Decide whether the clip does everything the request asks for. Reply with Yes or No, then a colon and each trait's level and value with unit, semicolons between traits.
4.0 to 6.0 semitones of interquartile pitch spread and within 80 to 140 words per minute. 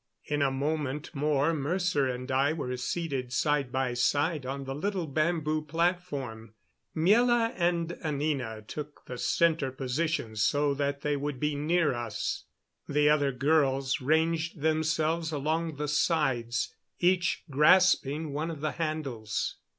No: average, 3.2 semitones; slow, 135 wpm